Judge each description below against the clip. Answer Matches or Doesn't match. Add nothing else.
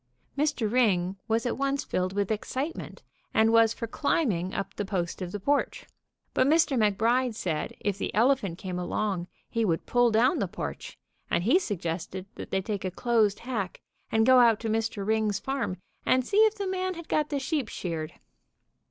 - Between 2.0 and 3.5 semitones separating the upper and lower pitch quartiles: Doesn't match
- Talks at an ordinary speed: Matches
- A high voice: Matches